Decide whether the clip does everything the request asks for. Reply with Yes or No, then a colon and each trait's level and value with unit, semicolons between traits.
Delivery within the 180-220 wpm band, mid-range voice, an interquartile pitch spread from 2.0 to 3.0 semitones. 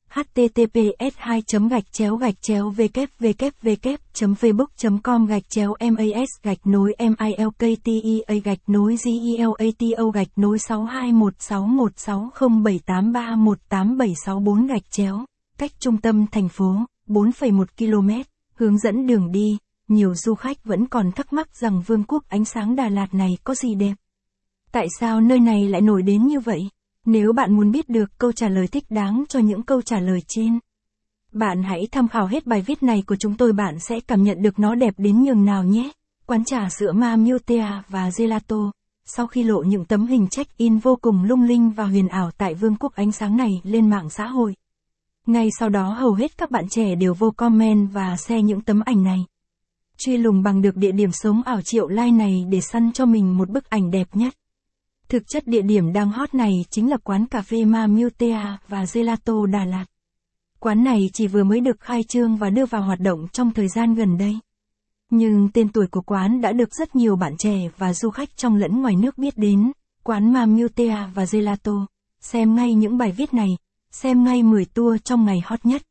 No: average, 200 wpm; high, 220 Hz; average, 2.7 semitones